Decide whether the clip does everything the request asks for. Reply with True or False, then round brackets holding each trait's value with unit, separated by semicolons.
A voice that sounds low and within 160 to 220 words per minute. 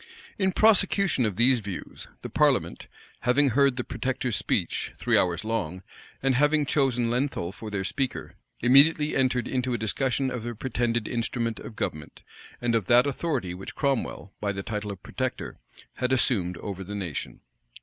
True (120 Hz; 165 wpm)